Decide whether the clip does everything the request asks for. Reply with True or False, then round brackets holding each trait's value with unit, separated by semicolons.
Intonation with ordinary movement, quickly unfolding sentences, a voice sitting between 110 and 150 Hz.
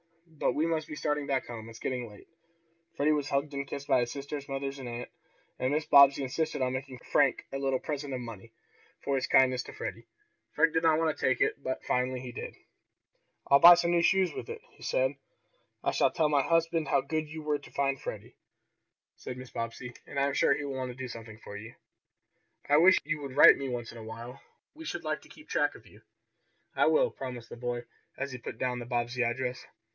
True (3.4 semitones; 230 wpm; 135 Hz)